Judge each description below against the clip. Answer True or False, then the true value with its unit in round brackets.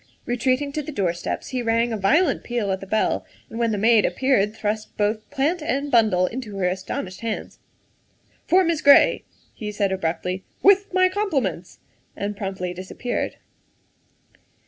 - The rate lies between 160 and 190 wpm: True (170 wpm)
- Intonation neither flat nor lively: False (6.0 semitones)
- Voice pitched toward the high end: True (220 Hz)